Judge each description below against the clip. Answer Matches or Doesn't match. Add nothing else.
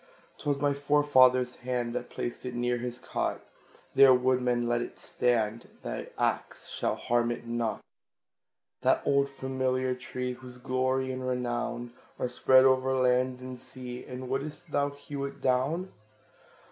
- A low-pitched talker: Matches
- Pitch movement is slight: Matches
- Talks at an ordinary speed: Matches